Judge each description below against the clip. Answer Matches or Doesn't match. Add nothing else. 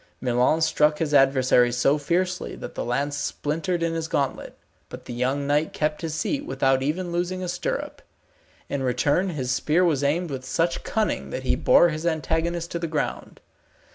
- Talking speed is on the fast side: Doesn't match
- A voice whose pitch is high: Doesn't match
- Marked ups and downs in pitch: Doesn't match